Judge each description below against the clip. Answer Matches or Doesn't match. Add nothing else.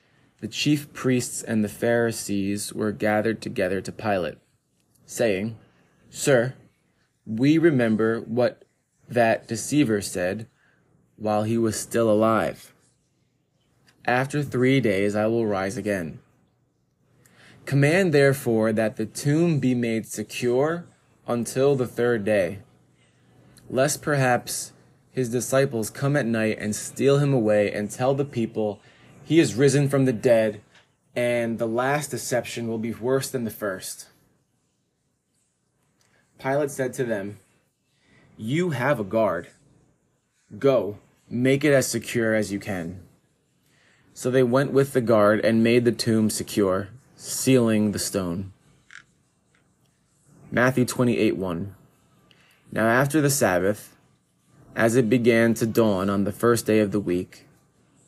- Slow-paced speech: Matches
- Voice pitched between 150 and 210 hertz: Doesn't match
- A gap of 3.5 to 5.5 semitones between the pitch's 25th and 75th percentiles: Matches